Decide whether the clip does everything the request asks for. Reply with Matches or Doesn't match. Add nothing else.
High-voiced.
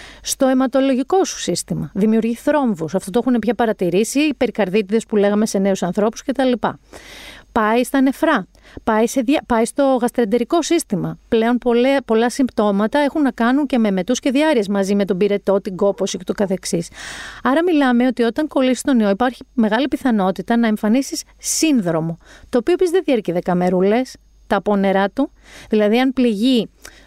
Matches